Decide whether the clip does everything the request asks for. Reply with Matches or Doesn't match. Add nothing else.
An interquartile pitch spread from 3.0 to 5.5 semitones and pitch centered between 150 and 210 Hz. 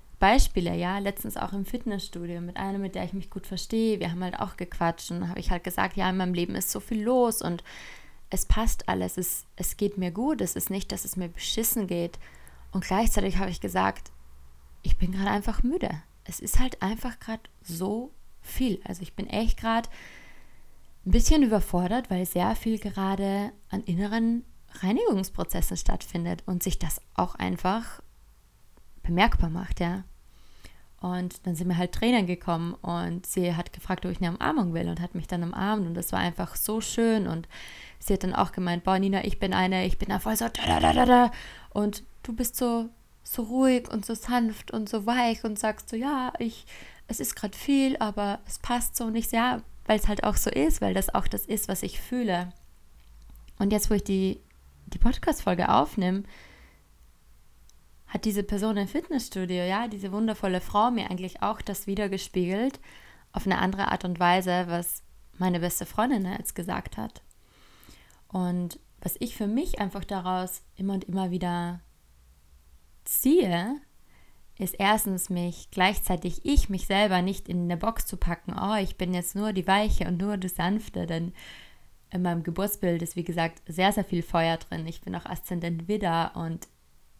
Matches